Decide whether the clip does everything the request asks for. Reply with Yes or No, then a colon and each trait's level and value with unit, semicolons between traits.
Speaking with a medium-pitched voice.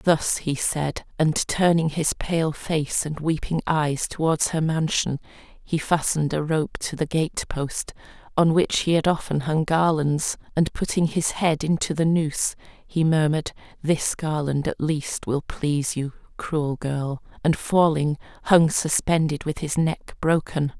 Yes: medium, 155 Hz